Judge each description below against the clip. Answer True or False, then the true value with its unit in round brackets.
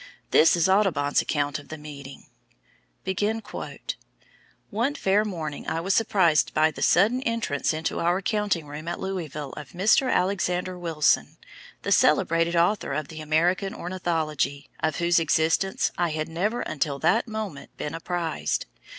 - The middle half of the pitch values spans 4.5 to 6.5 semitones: False (3.8 semitones)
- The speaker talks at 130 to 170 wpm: True (140 wpm)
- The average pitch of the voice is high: False (170 Hz)